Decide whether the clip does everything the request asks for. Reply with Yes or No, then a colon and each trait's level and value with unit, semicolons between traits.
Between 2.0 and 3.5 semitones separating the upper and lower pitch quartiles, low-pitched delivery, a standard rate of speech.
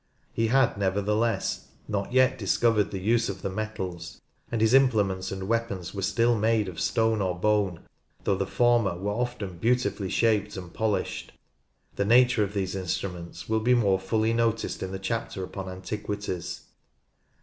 Yes: average, 3.2 semitones; low, 105 Hz; average, 160 wpm